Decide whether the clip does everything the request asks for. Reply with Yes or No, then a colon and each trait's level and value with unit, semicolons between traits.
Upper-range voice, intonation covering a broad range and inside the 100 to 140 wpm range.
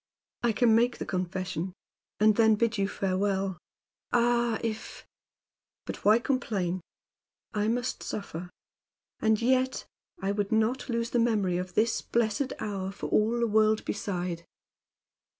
No: high, 215 Hz; average, 3.3 semitones; slow, 135 wpm